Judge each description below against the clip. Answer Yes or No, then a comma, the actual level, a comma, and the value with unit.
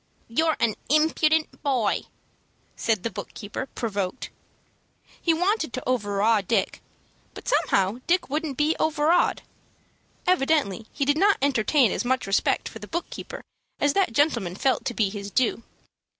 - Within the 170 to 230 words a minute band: No, average, 150 wpm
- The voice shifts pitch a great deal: Yes, wide, 6.5 semitones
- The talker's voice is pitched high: Yes, very high, 260 Hz